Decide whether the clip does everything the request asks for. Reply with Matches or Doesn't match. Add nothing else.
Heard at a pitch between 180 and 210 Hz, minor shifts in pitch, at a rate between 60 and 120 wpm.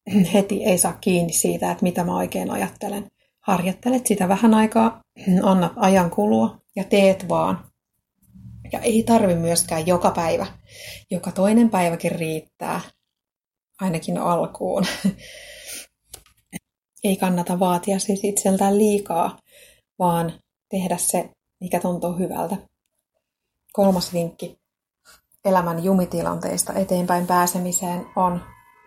Matches